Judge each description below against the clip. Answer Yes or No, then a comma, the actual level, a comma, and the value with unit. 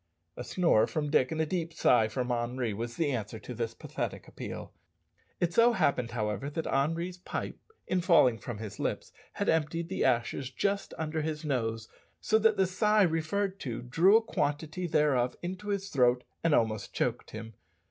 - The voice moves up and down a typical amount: No, wide, 6.7 semitones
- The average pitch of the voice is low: No, medium, 150 Hz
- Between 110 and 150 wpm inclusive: No, average, 180 wpm